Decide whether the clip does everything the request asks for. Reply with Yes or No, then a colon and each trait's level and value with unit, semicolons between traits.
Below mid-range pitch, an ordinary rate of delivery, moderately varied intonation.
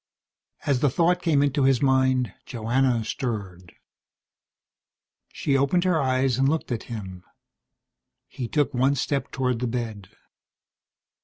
No: low, 130 Hz; slow, 130 wpm; average, 3.1 semitones